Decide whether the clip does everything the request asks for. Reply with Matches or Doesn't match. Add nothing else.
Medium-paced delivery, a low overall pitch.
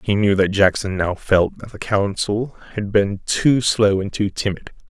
Matches